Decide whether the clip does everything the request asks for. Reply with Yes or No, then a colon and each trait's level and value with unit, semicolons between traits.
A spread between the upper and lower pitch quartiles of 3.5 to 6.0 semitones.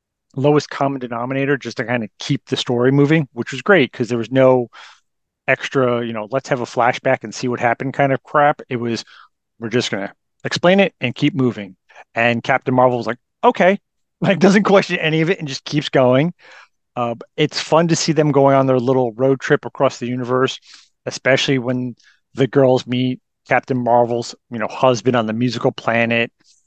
No: average, 3.0 semitones